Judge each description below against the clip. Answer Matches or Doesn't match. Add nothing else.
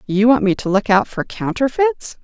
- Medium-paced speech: Doesn't match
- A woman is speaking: Matches